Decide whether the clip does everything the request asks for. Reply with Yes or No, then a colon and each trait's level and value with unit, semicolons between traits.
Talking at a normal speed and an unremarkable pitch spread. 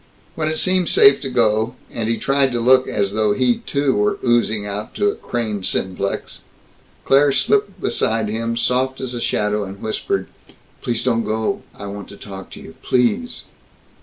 Yes: average, 180 wpm; average, 4.0 semitones